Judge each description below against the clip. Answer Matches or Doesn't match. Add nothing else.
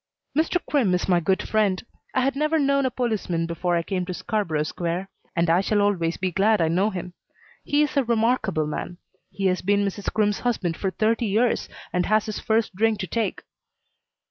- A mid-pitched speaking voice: Doesn't match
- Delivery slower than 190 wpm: Doesn't match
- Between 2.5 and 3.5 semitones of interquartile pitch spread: Doesn't match